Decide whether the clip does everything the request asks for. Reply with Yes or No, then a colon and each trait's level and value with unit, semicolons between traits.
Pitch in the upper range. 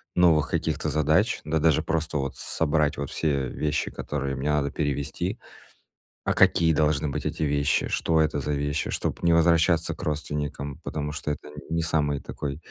No: very low, 75 Hz